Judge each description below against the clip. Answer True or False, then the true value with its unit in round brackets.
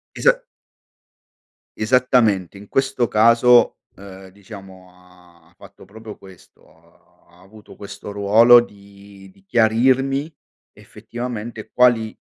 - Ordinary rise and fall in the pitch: True (3.7 semitones)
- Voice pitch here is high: False (105 Hz)